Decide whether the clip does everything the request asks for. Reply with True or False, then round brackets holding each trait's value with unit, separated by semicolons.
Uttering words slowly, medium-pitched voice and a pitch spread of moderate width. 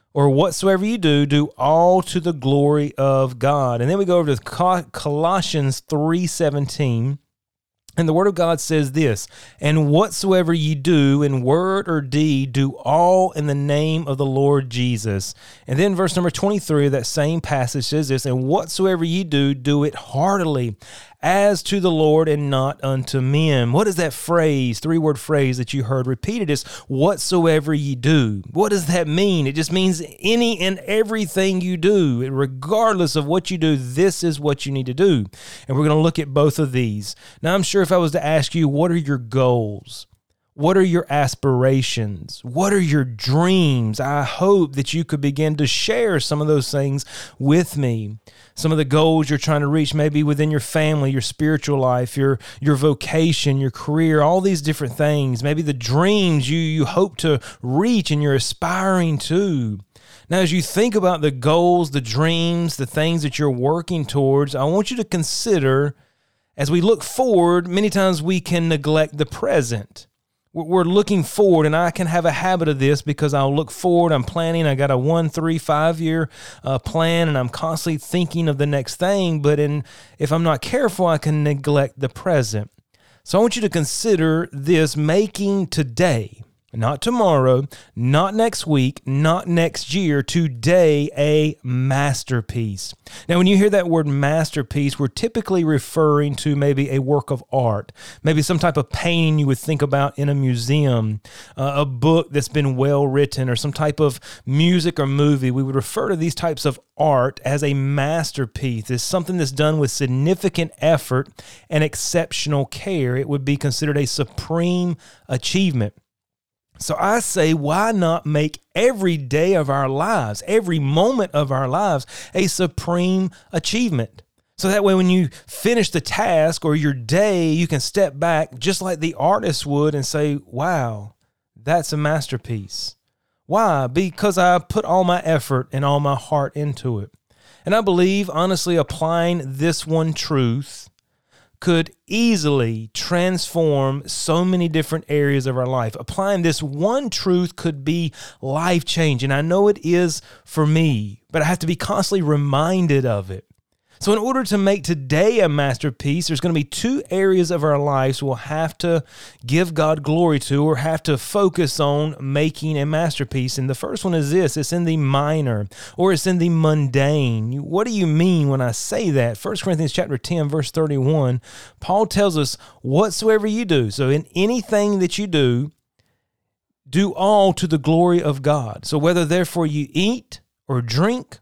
False (180 wpm; 150 Hz; 4.2 semitones)